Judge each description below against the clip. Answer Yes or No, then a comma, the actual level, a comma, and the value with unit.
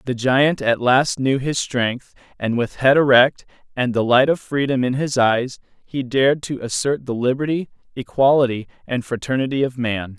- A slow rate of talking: No, average, 175 wpm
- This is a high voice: No, low, 130 Hz